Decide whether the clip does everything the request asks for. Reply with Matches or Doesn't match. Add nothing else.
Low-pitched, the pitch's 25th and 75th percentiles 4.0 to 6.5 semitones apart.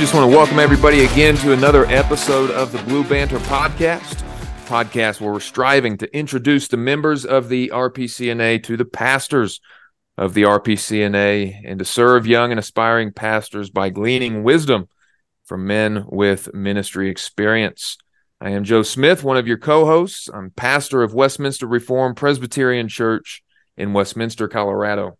Matches